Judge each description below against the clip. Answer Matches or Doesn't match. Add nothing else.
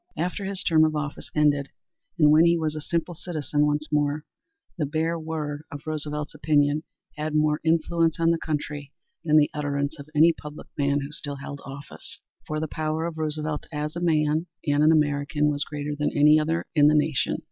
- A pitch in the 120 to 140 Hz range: Doesn't match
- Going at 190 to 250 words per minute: Matches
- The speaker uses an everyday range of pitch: Doesn't match